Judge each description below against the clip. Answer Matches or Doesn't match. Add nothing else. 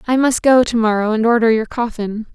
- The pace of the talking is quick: Matches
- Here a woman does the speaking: Matches